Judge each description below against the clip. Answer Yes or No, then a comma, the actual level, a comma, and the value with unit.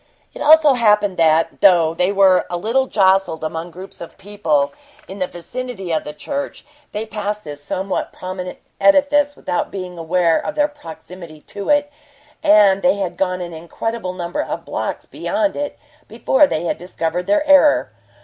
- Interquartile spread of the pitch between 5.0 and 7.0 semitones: Yes, average, 5.3 semitones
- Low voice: No, high, 190 Hz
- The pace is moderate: Yes, average, 165 wpm